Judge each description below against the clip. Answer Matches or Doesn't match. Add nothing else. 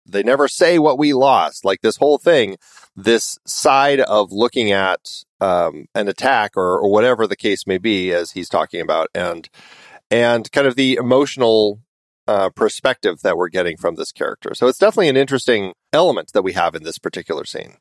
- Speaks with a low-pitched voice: Matches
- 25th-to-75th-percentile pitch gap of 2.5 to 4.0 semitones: Doesn't match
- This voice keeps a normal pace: Matches